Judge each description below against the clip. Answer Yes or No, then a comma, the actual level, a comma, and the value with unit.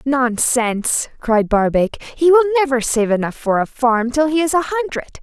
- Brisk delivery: No, average, 185 wpm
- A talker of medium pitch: No, very high, 255 Hz